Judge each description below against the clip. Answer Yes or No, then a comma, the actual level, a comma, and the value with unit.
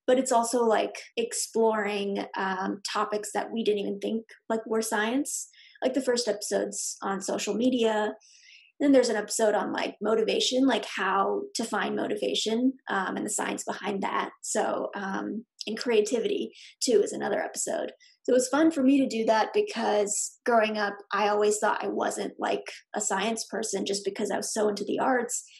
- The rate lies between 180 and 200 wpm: Yes, average, 185 wpm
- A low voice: No, high, 225 Hz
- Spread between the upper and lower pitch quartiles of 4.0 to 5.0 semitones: No, average, 3.6 semitones